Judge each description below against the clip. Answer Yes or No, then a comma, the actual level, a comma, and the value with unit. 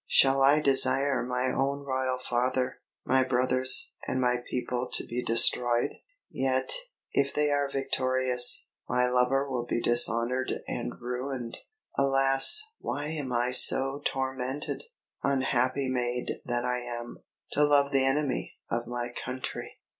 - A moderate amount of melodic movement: No, narrow, 1.6 semitones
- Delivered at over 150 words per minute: No, slow, 135 wpm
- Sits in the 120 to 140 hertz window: Yes, low, 130 Hz